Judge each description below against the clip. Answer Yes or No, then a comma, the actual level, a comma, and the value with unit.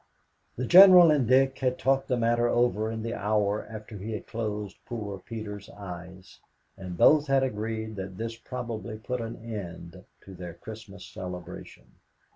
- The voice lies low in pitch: Yes, low, 110 Hz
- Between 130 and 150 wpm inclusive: No, average, 160 wpm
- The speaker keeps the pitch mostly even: No, average, 3.4 semitones